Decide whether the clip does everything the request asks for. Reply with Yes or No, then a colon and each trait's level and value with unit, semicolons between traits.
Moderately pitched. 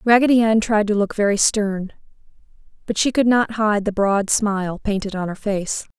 No: high, 210 Hz